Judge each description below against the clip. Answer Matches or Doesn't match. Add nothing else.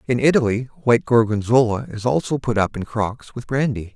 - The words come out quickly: Doesn't match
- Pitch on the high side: Doesn't match